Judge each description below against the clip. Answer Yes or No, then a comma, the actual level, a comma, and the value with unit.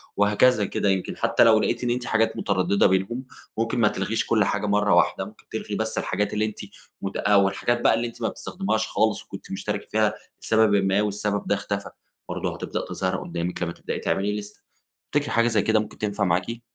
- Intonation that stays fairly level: Yes, narrow, 2.2 semitones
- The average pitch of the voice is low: Yes, low, 105 Hz